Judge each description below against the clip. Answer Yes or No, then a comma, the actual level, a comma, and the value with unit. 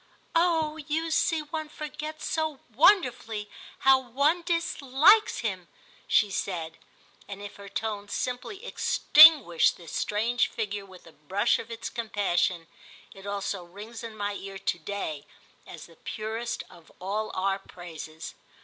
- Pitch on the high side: Yes, high, 215 Hz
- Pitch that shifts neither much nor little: No, wide, 7.6 semitones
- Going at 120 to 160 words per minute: Yes, average, 140 wpm